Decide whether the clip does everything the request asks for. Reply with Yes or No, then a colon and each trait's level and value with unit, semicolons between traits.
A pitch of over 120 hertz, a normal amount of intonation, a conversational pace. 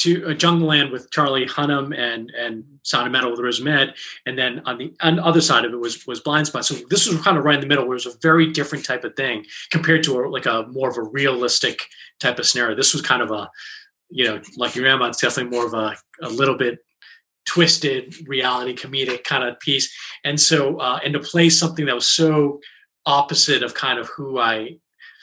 No: medium, 140 Hz; average, 4.2 semitones; fast, 235 wpm